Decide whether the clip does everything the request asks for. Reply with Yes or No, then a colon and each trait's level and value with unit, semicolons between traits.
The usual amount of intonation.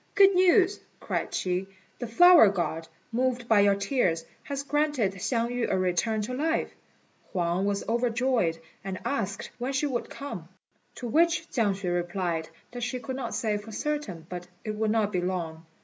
No: wide, 6.1 semitones